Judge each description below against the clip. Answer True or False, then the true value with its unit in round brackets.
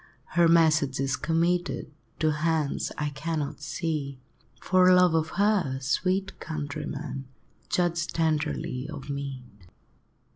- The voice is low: False (155 Hz)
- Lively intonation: False (3.1 semitones)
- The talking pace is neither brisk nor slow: False (110 wpm)